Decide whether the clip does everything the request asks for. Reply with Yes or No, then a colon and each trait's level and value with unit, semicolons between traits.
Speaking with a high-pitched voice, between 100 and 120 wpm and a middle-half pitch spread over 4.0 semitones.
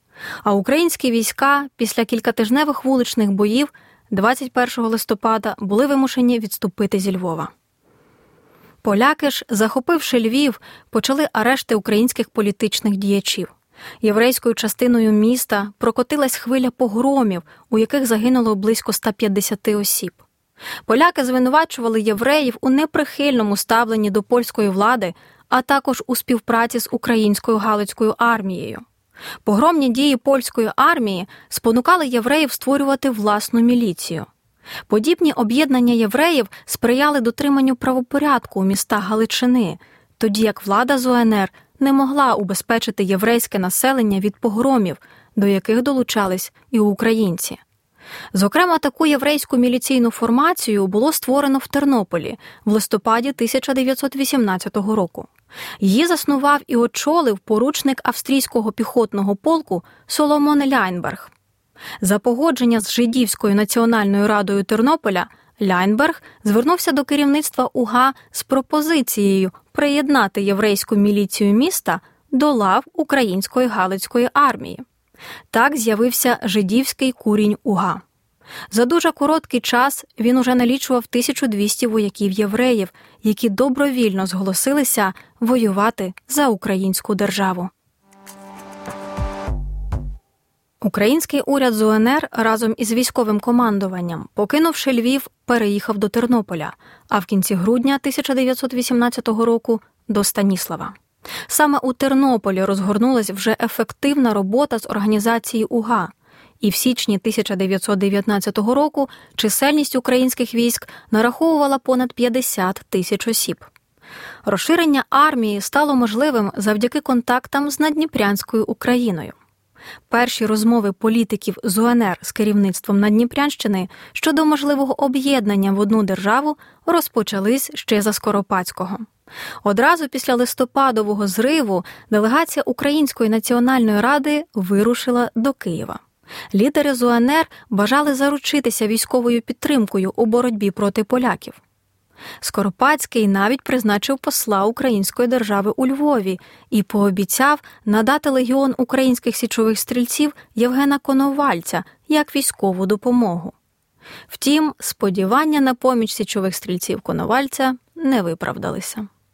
Yes: high, 235 Hz; slow, 105 wpm; average, 4.4 semitones